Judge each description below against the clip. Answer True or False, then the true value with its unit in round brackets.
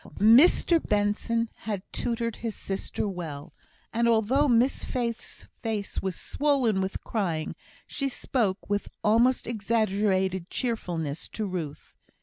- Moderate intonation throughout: True (3.6 semitones)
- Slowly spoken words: True (120 wpm)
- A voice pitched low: False (215 Hz)